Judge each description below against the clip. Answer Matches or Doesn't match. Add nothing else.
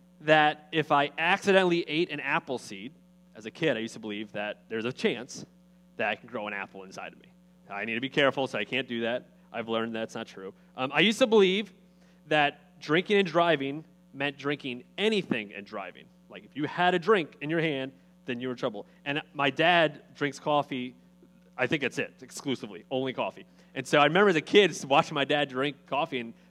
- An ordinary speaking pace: Doesn't match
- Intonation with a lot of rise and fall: Matches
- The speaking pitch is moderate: Matches